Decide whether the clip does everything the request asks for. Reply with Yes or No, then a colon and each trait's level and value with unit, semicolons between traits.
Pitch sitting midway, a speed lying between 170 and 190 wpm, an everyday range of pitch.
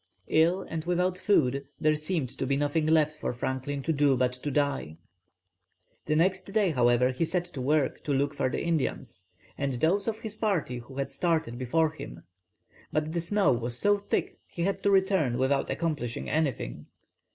Yes: medium, 150 Hz; average, 185 wpm; average, 4.9 semitones